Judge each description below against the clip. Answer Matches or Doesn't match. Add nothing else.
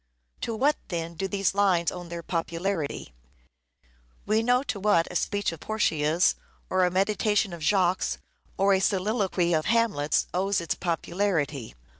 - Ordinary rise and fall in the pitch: Matches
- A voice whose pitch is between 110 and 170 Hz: Doesn't match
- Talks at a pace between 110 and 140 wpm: Doesn't match